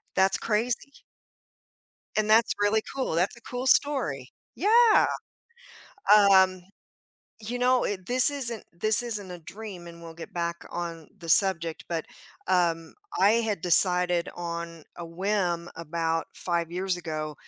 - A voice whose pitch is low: No, medium, 180 Hz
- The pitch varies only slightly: No, average, 4.4 semitones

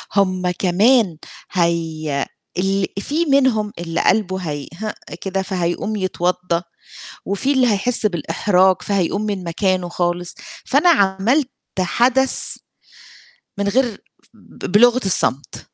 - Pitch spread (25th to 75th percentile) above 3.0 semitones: Yes, average, 3.7 semitones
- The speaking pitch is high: Yes, high, 195 Hz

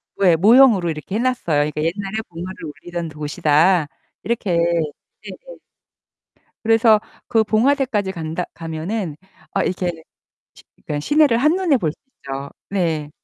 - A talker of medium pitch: Yes, medium, 180 Hz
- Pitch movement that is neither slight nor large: No, wide, 5.9 semitones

